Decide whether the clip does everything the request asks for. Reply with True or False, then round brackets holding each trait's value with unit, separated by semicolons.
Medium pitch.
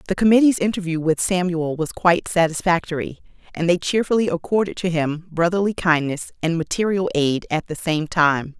True (170 Hz)